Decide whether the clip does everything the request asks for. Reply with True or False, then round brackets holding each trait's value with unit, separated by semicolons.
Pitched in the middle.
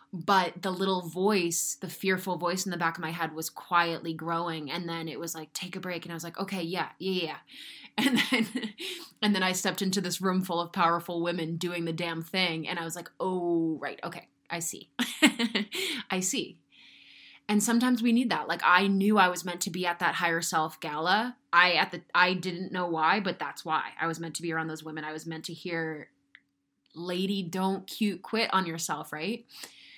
True (180 Hz)